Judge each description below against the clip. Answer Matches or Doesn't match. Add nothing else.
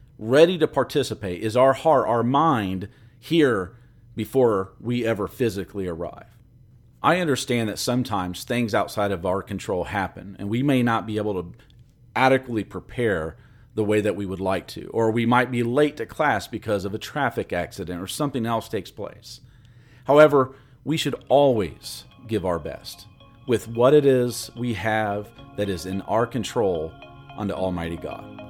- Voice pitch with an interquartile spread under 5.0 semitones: Matches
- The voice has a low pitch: Matches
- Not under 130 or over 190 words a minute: Matches